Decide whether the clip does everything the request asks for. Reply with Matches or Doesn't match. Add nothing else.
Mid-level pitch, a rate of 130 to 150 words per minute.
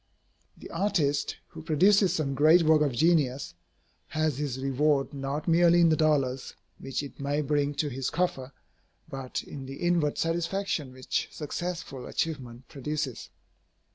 Matches